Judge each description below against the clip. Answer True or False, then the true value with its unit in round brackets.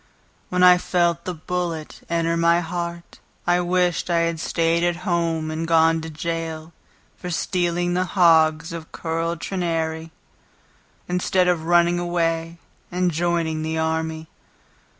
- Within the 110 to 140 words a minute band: True (135 wpm)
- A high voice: False (170 Hz)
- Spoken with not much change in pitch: True (1.4 semitones)